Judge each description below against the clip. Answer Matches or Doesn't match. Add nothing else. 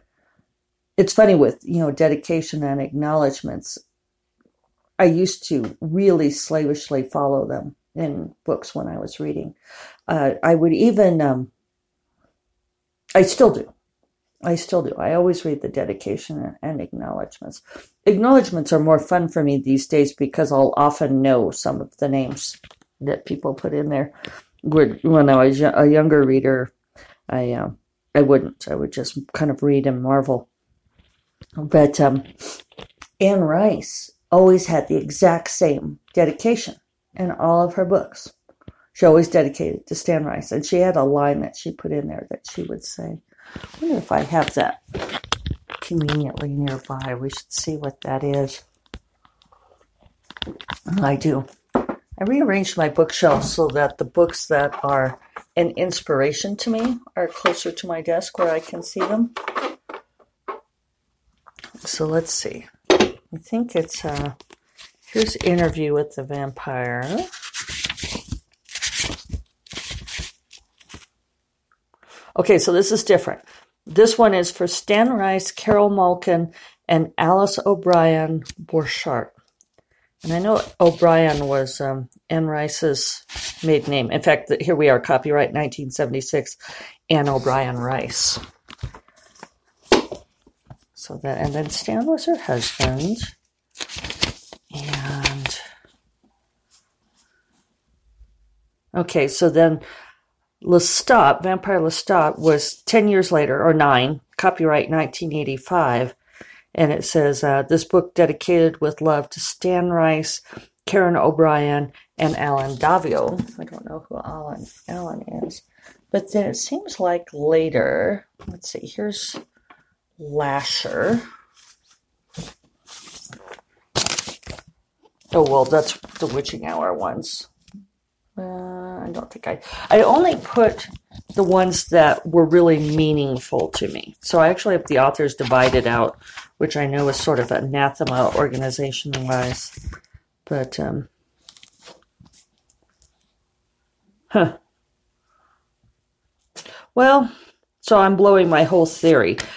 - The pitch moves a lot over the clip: Doesn't match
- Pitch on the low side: Doesn't match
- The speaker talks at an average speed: Doesn't match